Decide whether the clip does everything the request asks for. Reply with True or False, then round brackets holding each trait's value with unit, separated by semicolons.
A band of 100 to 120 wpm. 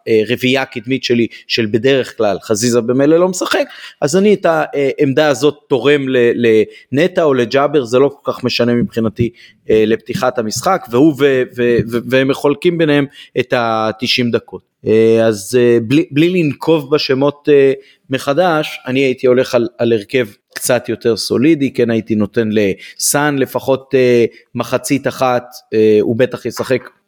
False (135 wpm)